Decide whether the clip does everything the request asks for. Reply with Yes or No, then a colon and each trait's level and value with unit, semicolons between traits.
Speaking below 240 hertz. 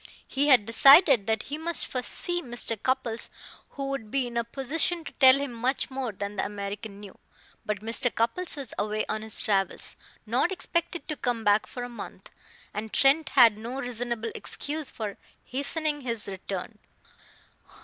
No: high, 245 Hz